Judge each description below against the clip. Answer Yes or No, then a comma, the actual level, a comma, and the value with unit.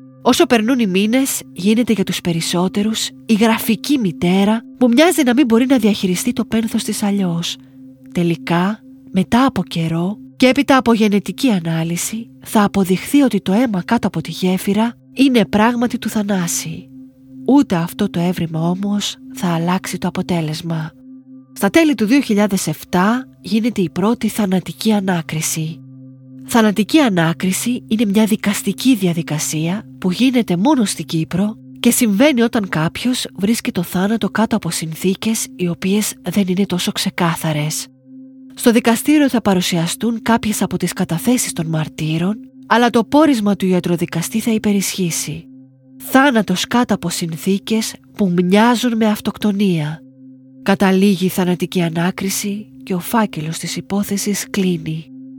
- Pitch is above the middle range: Yes, high, 200 Hz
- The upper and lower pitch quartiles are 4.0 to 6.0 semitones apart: Yes, average, 5.1 semitones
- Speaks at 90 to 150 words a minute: Yes, average, 135 wpm